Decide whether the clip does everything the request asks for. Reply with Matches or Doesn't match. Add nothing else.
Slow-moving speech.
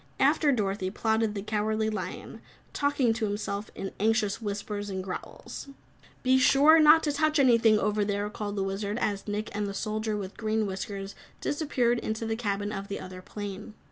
Doesn't match